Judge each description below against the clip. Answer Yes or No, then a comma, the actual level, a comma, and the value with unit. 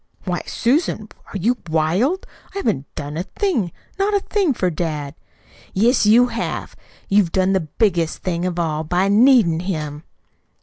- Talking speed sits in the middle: Yes, average, 160 wpm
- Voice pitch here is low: No, medium, 185 Hz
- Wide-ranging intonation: Yes, wide, 6.5 semitones